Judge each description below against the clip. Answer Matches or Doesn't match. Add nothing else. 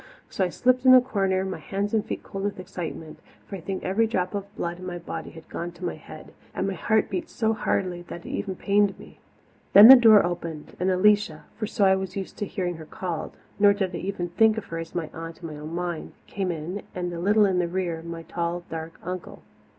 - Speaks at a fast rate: Matches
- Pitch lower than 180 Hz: Doesn't match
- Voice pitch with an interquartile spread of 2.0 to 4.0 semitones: Matches